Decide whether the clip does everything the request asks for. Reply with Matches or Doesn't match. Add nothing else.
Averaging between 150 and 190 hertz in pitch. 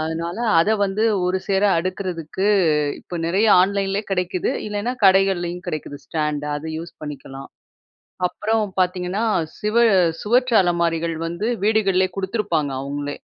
Matches